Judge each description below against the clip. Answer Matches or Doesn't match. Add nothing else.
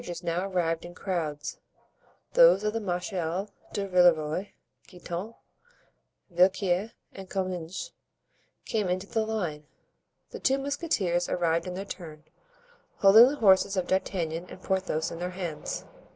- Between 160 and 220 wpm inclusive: Doesn't match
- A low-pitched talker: Doesn't match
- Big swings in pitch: Doesn't match